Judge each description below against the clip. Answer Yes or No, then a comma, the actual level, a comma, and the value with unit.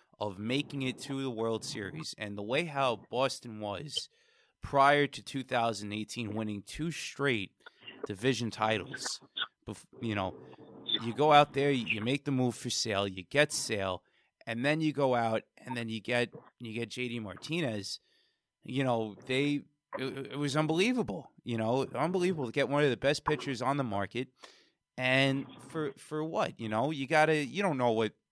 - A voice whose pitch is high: No, low, 130 Hz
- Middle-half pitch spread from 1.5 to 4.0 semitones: No, average, 4.4 semitones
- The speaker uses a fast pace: No, average, 175 wpm